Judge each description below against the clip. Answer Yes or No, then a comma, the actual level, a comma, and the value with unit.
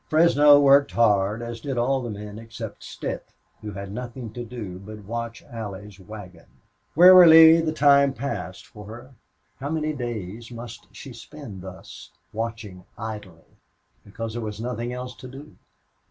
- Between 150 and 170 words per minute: Yes, average, 155 wpm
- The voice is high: No, low, 115 Hz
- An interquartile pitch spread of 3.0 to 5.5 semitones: Yes, average, 4.6 semitones